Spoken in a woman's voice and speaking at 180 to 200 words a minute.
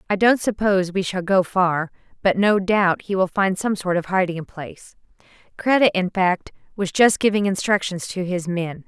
Yes: female; average, 190 wpm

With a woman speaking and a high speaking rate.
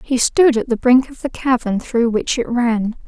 Yes: female; fast, 235 wpm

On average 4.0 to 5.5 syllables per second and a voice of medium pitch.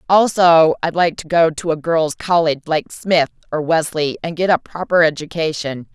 Yes: 5.1 syllables/s; medium, 160 Hz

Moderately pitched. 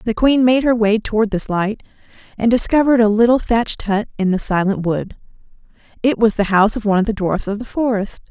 No: high, 220 Hz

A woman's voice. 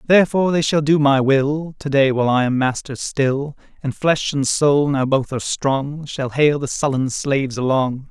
No: male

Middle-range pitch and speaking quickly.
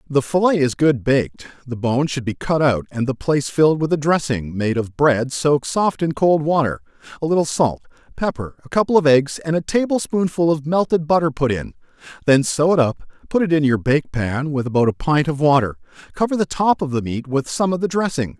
Yes: medium, 145 Hz; fast, 225 wpm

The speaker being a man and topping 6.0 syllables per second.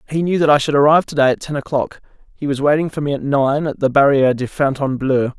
Yes: male; 6.7 syllables/s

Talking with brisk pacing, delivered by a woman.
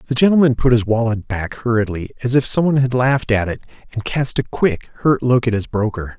No: fast, 235 wpm; male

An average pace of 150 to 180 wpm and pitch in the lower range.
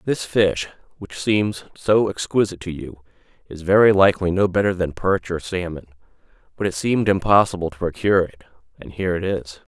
Yes: average, 170 wpm; very low, 95 Hz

